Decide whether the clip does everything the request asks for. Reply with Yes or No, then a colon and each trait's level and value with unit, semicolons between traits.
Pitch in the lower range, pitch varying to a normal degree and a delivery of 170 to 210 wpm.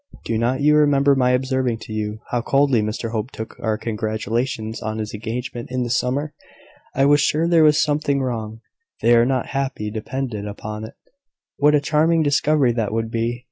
Yes: low, 125 Hz; average, 4.1 semitones; average, 185 wpm